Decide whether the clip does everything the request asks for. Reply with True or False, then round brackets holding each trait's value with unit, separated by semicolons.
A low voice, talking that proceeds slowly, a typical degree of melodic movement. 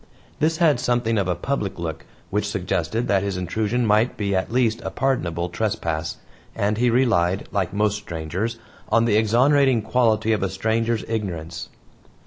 False (110 Hz; 160 wpm; 4.0 semitones)